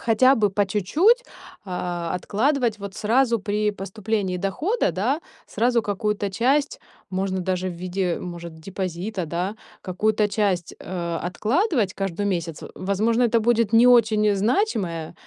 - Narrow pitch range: No, average, 4.0 semitones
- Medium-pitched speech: No, high, 205 Hz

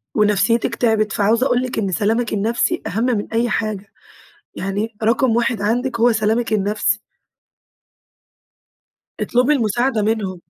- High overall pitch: Yes, high, 220 Hz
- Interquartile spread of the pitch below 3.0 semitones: Yes, narrow, 2.4 semitones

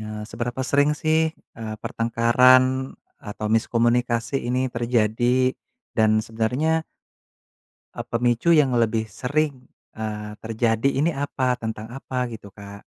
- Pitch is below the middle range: Yes, low, 120 Hz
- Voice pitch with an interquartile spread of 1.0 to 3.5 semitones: Yes, average, 2.9 semitones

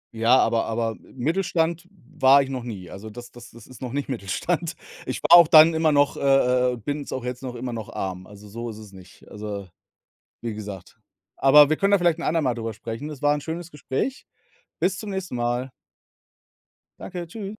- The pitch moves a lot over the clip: Yes, wide, 5.9 semitones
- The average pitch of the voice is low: Yes, low, 130 Hz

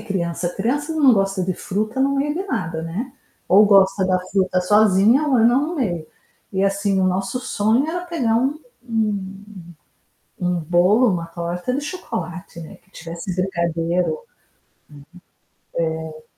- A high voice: Yes, high, 195 Hz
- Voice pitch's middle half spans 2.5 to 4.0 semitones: No, wide, 5.4 semitones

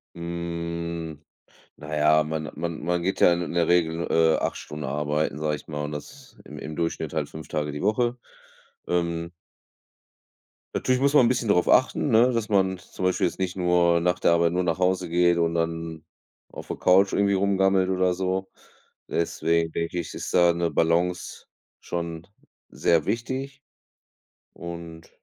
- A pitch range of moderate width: No, narrow, 2.2 semitones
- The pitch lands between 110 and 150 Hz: No, very low, 85 Hz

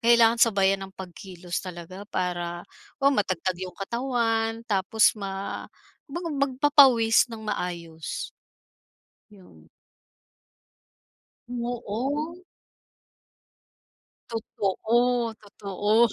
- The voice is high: Yes, high, 210 Hz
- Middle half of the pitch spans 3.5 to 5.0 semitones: Yes, average, 4.1 semitones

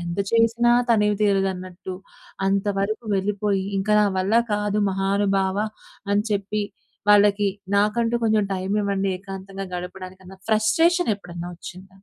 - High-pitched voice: Yes, high, 200 Hz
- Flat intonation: Yes, narrow, 1.7 semitones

